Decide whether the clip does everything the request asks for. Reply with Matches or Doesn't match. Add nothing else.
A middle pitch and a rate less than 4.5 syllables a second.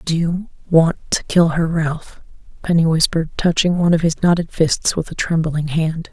Doesn't match